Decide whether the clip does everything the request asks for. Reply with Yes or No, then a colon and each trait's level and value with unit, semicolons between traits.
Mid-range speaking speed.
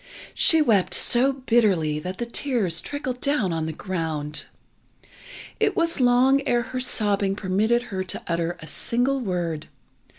Yes: average, 145 wpm